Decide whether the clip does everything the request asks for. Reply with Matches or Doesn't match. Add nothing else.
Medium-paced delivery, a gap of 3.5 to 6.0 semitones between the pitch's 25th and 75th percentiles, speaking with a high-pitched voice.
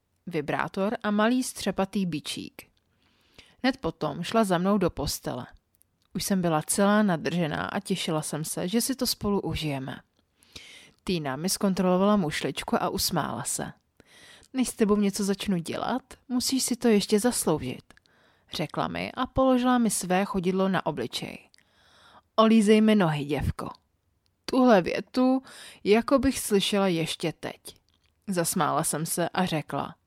Matches